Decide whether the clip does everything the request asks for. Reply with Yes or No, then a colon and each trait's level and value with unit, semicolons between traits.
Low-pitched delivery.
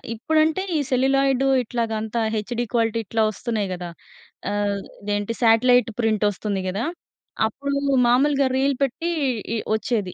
No: high, 230 Hz